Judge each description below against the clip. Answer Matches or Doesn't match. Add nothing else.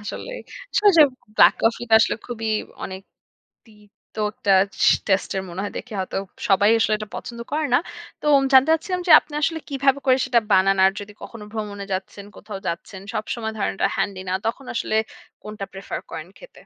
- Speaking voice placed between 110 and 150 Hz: Doesn't match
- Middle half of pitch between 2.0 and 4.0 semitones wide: Doesn't match